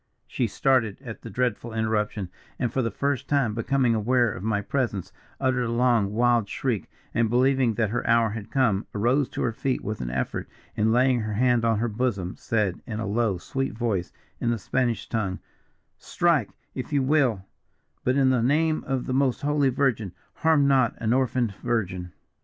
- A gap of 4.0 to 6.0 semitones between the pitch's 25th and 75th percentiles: No, average, 3.2 semitones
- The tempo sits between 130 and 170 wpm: No, average, 185 wpm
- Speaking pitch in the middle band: No, low, 120 Hz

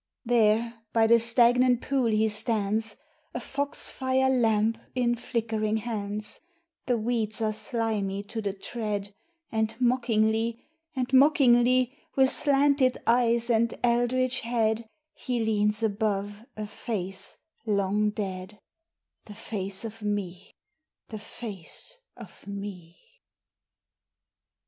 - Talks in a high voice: Yes, high, 225 Hz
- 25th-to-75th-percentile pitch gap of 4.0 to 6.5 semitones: No, narrow, 2.5 semitones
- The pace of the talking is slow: Yes, slow, 115 wpm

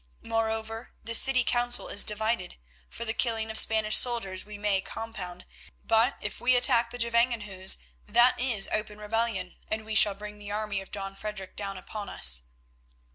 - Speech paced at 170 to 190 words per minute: Yes, average, 175 wpm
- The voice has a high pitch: Yes, high, 215 Hz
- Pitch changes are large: No, narrow, 2.4 semitones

